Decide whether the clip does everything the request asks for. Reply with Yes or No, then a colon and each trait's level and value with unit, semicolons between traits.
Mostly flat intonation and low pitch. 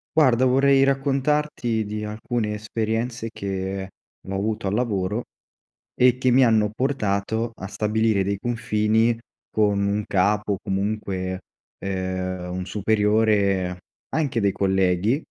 No: average, 3.3 semitones; low, 105 Hz